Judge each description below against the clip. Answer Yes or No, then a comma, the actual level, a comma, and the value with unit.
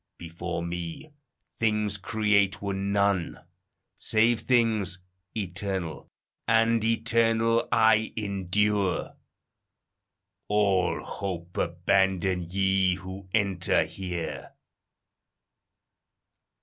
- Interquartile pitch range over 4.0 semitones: No, average, 3.0 semitones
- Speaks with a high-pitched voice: No, low, 100 Hz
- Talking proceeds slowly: Yes, slow, 70 wpm